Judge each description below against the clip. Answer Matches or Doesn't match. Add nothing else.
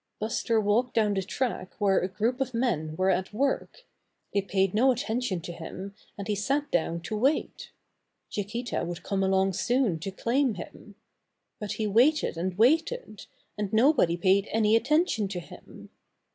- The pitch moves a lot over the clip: Doesn't match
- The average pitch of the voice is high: Matches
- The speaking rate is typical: Matches